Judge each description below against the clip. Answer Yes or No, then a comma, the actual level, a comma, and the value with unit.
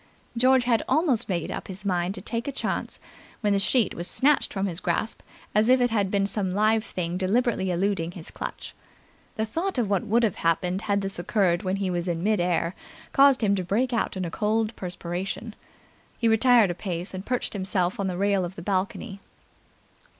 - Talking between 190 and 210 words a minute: Yes, fast, 205 wpm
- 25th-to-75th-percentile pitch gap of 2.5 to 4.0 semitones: Yes, average, 3.7 semitones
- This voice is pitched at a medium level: No, high, 200 Hz